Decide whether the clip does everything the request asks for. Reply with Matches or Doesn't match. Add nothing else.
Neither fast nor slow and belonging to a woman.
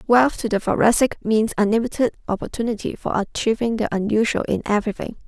Matches